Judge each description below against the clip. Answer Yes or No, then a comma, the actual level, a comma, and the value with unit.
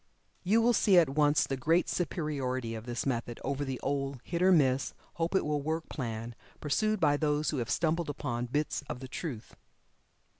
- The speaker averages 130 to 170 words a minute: No, average, 190 wpm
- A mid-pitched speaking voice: Yes, medium, 145 Hz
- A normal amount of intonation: Yes, average, 4.1 semitones